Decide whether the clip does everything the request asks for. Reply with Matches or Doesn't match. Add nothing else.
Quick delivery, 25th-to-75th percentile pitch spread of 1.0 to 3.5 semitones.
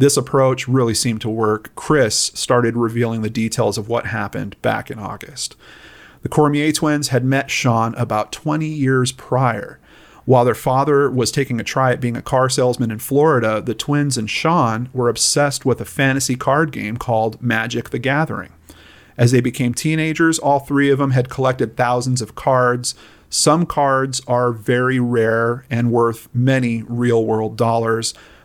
Doesn't match